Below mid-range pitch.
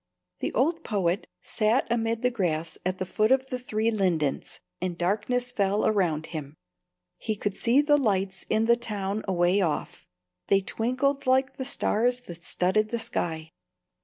No: high, 215 Hz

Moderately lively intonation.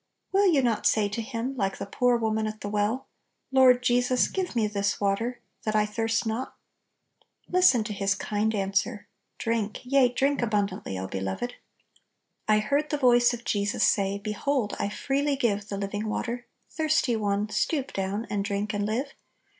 Yes: average, 3.5 semitones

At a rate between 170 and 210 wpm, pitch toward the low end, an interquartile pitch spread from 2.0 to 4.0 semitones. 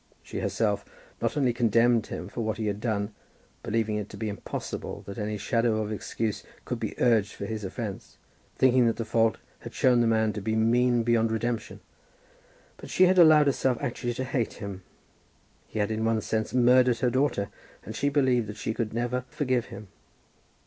Yes: average, 190 wpm; low, 115 Hz; narrow, 2.4 semitones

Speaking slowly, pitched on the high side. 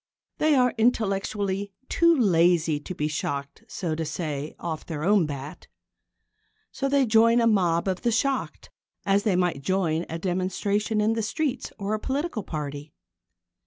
No: average, 160 wpm; high, 195 Hz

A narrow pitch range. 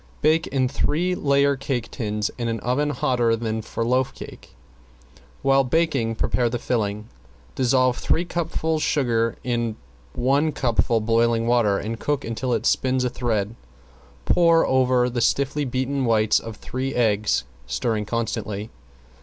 No: average, 3.2 semitones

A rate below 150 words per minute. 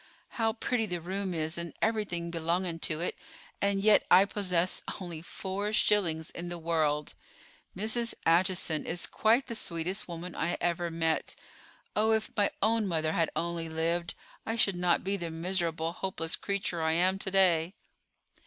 No: average, 160 wpm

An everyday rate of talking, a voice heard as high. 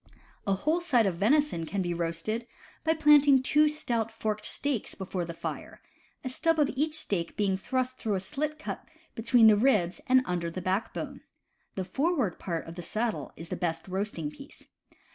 Yes: average, 180 wpm; high, 220 Hz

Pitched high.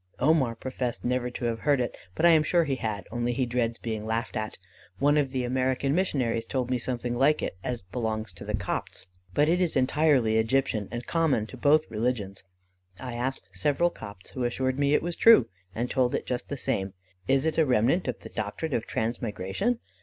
No: low, 125 Hz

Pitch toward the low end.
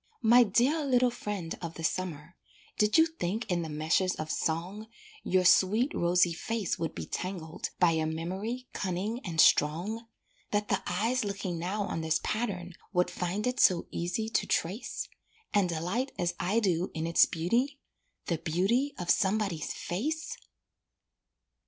No: medium, 185 Hz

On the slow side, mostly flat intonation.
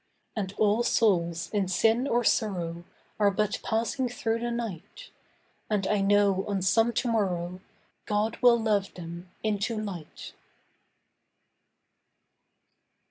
No: slow, 120 wpm; average, 3.1 semitones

